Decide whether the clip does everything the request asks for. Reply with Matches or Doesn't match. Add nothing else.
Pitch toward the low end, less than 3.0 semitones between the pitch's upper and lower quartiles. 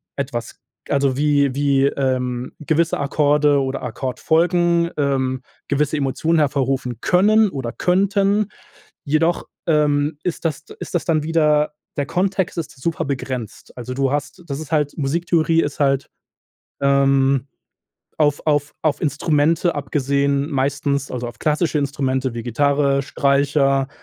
Doesn't match